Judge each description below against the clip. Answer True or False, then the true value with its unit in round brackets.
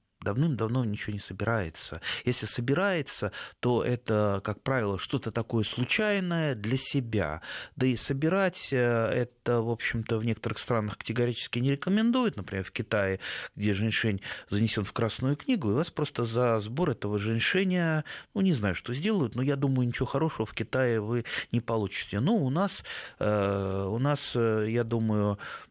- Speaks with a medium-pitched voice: False (120 Hz)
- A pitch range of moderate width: True (4.7 semitones)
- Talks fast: False (150 wpm)